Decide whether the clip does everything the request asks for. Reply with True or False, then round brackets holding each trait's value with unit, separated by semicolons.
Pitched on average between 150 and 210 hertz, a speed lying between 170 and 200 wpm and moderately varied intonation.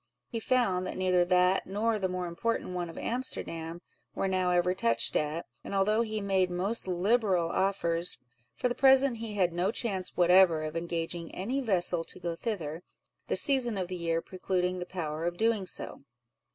True (185 Hz; 180 wpm; 3.5 semitones)